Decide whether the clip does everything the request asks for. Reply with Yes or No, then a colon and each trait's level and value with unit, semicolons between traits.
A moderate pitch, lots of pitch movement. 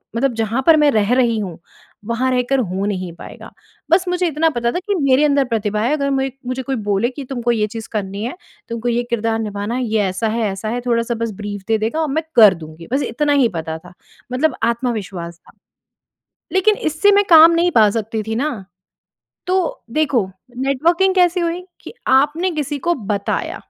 No: high, 240 Hz; wide, 5.7 semitones